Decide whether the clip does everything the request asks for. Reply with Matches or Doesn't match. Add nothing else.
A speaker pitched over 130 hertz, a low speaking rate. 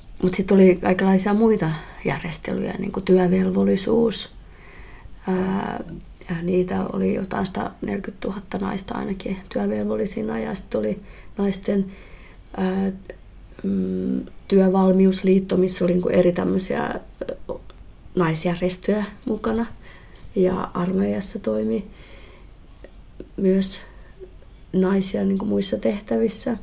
Matches